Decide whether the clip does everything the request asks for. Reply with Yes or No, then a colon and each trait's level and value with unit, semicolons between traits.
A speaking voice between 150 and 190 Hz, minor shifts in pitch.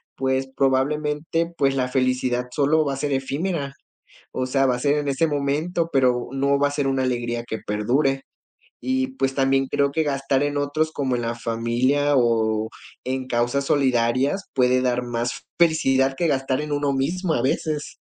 No: low, 135 Hz; narrow, 2.3 semitones